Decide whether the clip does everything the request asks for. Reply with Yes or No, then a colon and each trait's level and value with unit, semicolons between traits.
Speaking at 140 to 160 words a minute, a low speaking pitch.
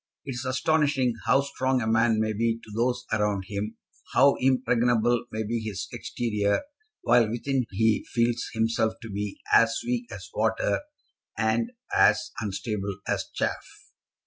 Yes: average, 145 wpm; low, 115 Hz